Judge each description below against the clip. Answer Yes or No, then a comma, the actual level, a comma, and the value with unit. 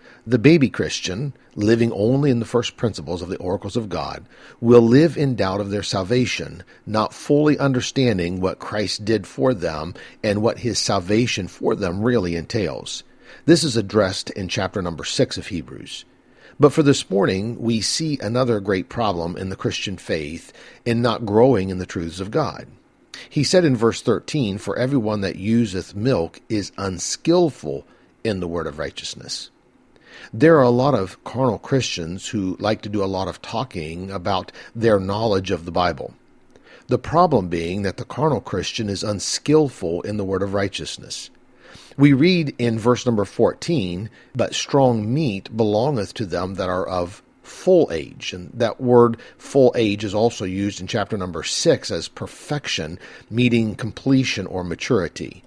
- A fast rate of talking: No, average, 165 wpm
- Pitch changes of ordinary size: Yes, average, 4.7 semitones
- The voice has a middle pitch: No, low, 110 Hz